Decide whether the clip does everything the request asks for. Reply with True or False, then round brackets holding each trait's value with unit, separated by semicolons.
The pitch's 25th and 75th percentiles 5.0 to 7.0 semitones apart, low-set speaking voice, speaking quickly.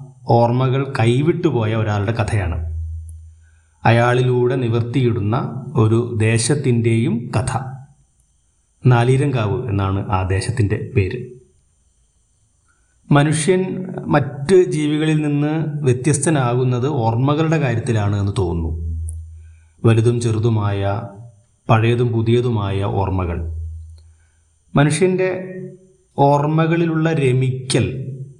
False (5.6 semitones; 120 Hz; 65 wpm)